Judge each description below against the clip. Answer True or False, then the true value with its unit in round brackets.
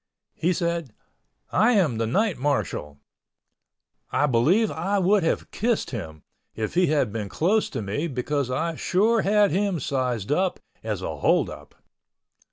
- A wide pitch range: True (7.7 semitones)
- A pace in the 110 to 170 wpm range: True (155 wpm)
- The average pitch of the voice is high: False (160 Hz)